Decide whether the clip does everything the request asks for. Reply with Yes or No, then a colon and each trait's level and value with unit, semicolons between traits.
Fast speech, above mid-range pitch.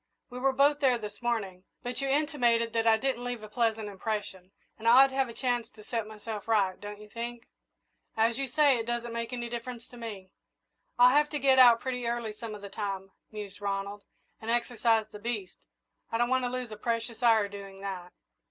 Yes: fast, 215 wpm; high, 230 Hz